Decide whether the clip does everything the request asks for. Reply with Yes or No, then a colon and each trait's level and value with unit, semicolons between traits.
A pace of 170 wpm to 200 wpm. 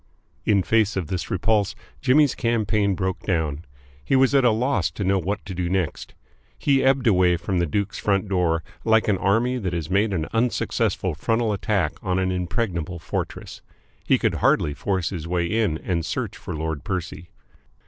Yes: average, 180 wpm